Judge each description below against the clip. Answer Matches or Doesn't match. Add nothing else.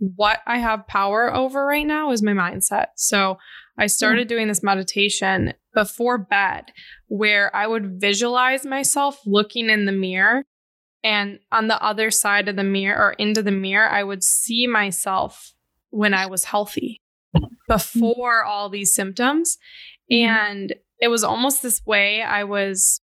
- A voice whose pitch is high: Matches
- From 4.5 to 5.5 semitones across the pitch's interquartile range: Doesn't match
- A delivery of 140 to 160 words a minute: Matches